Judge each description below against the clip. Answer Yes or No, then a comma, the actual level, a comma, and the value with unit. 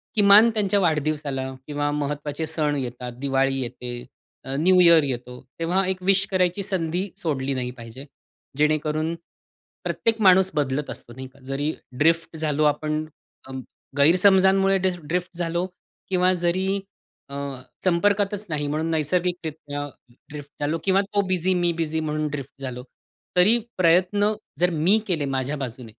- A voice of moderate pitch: Yes, medium, 160 Hz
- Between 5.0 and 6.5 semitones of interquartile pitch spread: No, average, 4.4 semitones